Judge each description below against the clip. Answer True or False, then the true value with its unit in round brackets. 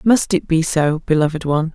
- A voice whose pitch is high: False (165 Hz)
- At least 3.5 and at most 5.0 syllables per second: False (5.5 syllables/s)